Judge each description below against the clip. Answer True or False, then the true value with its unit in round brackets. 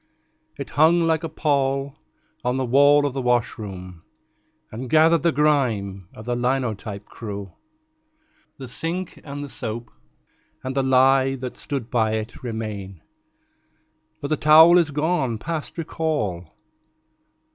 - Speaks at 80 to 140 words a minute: True (135 wpm)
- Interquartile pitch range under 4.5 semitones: False (5.3 semitones)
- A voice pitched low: True (130 Hz)